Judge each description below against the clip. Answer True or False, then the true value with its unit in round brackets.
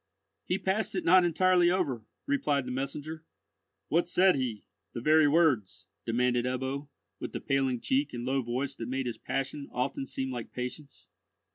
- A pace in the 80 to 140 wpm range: False (160 wpm)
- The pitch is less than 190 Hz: True (135 Hz)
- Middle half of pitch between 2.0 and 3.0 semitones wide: False (4.7 semitones)